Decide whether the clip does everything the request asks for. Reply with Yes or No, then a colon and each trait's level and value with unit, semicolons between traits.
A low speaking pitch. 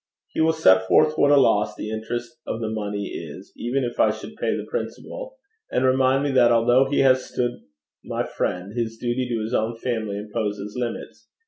Yes: low, 120 Hz